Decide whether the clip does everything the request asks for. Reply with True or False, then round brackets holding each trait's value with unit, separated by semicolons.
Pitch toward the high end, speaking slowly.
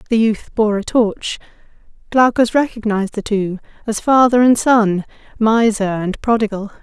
True (220 Hz; 130 wpm)